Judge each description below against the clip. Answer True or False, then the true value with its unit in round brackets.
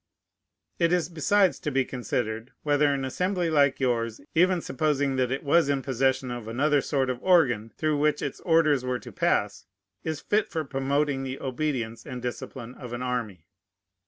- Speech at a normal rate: True (175 wpm)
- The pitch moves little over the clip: False (3.6 semitones)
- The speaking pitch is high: False (135 Hz)